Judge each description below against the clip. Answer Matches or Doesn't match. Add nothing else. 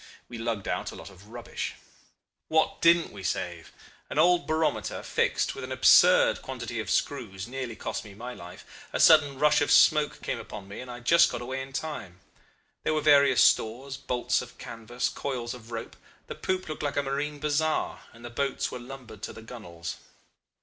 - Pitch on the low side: Matches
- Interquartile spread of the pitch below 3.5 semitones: Doesn't match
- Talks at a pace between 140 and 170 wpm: Doesn't match